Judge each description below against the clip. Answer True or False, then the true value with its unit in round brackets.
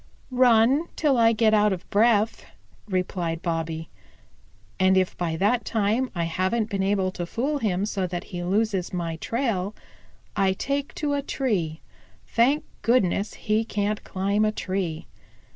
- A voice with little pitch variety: False (4.0 semitones)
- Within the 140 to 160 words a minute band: True (150 wpm)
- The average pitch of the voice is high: True (205 Hz)